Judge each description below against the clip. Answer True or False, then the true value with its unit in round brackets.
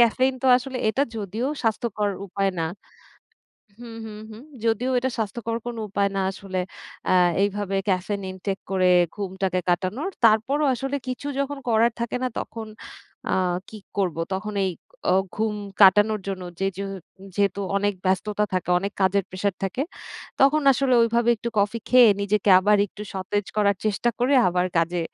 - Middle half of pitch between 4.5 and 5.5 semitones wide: False (3.4 semitones)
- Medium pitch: False (210 Hz)